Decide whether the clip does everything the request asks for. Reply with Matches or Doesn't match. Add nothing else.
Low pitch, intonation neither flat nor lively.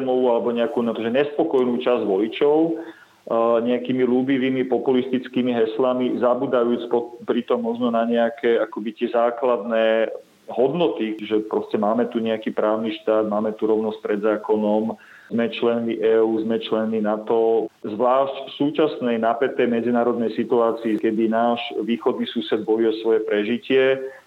Doesn't match